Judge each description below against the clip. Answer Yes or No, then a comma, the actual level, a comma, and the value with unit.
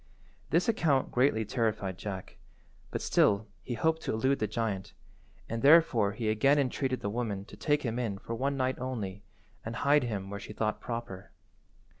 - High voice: No, low, 115 Hz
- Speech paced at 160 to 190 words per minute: Yes, average, 175 wpm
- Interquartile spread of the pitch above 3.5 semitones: Yes, average, 4.3 semitones